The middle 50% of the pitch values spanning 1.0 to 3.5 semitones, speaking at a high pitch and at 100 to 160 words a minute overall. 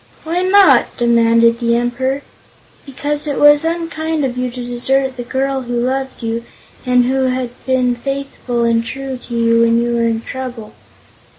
No: narrow, 2.5 semitones; very high, 250 Hz; average, 170 wpm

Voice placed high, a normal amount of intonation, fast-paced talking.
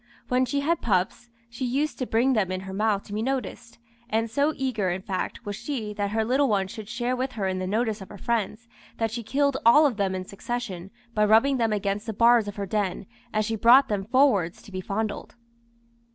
Yes: high, 220 Hz; average, 3.5 semitones; fast, 225 wpm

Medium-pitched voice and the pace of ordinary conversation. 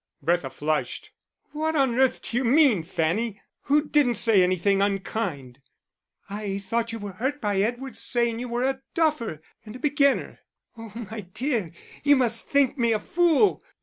No: high, 230 Hz; average, 165 wpm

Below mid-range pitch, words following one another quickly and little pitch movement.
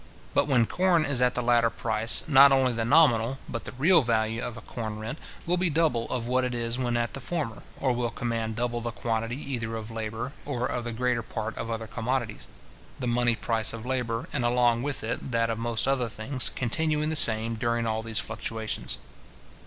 Yes: low, 120 Hz; fast, 210 wpm; narrow, 2.2 semitones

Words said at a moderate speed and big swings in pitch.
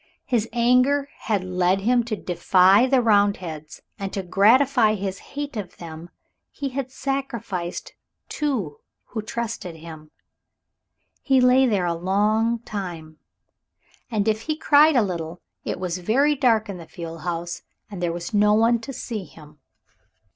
Yes: average, 155 wpm; wide, 5.7 semitones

